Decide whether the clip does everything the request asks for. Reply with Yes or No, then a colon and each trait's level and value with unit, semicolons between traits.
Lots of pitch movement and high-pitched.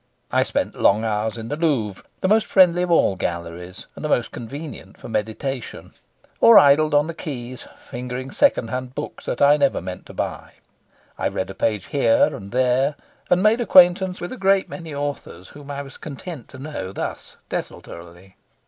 No: wide, 6.9 semitones; low, 135 Hz